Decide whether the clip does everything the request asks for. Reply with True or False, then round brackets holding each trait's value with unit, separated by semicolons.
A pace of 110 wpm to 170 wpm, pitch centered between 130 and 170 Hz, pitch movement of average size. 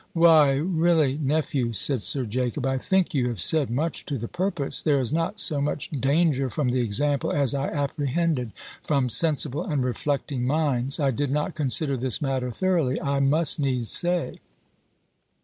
True (165 wpm; 140 Hz; 3.5 semitones)